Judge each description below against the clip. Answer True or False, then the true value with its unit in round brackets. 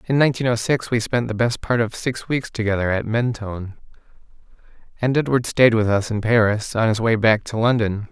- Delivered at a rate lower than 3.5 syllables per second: False (5.5 syllables/s)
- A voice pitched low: True (115 Hz)